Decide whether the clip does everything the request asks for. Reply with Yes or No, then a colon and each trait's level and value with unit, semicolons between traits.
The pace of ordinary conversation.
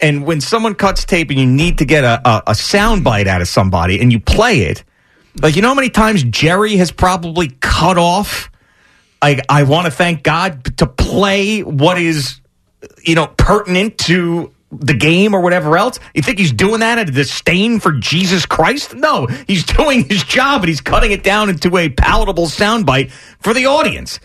Yes: average, 195 wpm